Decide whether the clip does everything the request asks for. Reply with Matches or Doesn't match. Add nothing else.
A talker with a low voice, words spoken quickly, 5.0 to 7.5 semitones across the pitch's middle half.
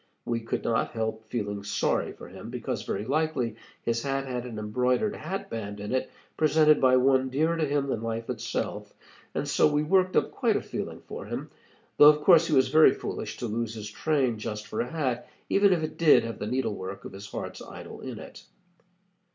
Matches